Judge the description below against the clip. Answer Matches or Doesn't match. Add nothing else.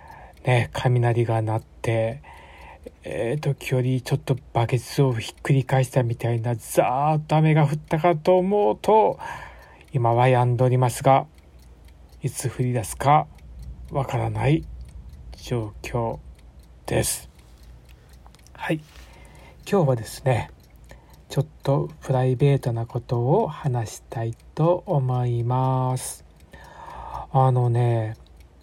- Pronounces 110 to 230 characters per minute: Matches